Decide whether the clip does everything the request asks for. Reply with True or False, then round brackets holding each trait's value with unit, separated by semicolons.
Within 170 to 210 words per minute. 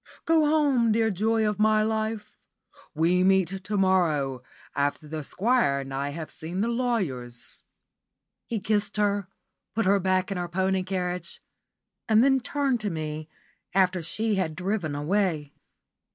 False (150 wpm)